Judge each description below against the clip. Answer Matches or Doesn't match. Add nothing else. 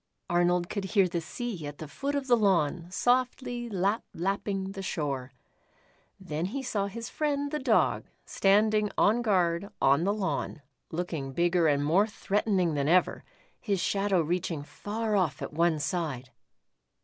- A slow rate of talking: Doesn't match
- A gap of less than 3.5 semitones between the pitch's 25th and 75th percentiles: Doesn't match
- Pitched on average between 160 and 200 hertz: Matches